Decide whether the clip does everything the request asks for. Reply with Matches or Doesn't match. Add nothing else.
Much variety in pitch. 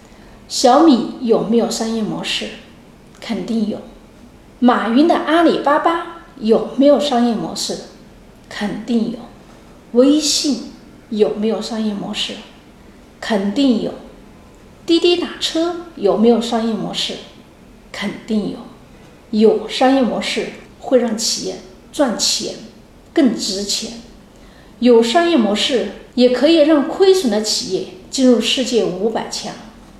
Doesn't match